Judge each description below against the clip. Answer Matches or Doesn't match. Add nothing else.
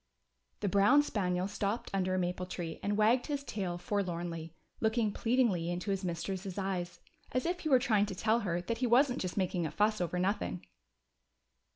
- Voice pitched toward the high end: Matches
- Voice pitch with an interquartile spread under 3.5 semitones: Doesn't match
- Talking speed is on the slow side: Doesn't match